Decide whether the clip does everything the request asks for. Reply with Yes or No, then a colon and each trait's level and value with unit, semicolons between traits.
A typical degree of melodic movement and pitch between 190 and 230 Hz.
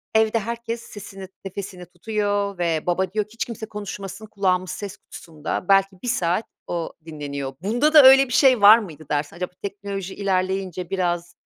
Yes: average, 3.4 semitones; high, 195 Hz